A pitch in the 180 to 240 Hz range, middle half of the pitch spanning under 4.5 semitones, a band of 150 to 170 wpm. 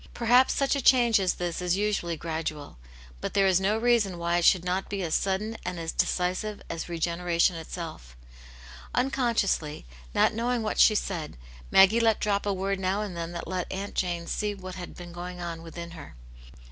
No: medium, 185 Hz; average, 3.6 semitones; average, 190 wpm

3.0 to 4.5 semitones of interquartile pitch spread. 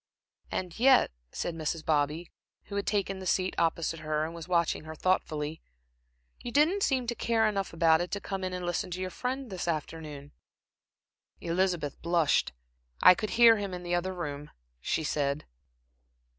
Yes: average, 3.8 semitones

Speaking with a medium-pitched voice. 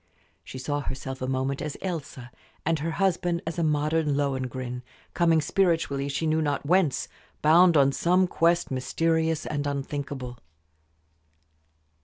Yes: medium, 150 Hz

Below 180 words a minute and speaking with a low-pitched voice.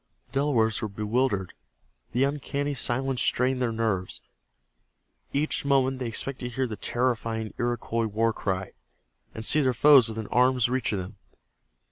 Yes: average, 150 wpm; low, 120 Hz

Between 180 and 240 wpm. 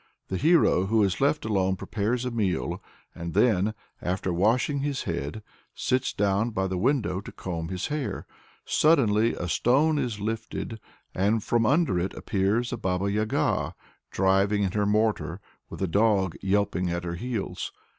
No: average, 160 wpm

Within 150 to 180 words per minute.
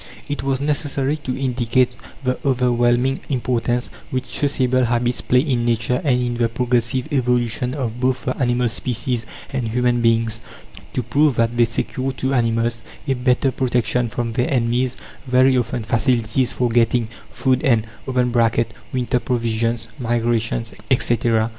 No: average, 140 wpm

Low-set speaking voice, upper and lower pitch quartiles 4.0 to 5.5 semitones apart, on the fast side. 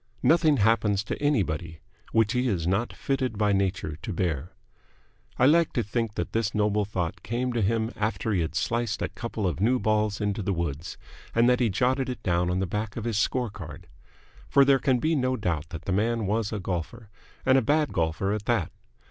Yes: low, 105 Hz; average, 4.4 semitones; fast, 210 wpm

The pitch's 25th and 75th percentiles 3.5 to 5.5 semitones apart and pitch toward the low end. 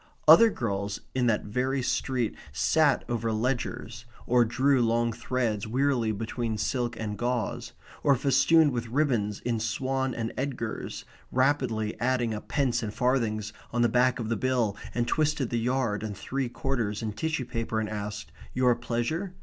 No: average, 2.9 semitones; low, 120 Hz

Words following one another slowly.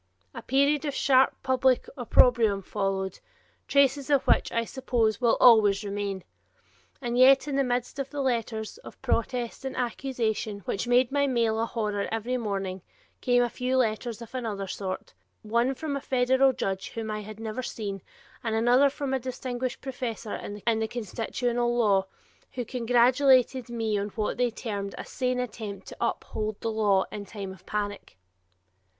No: average, 165 wpm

